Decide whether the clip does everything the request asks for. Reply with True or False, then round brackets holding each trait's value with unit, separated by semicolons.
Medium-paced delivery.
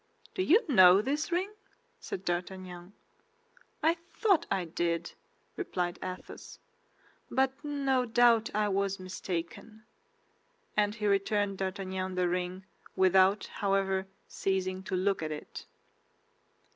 False (115 wpm)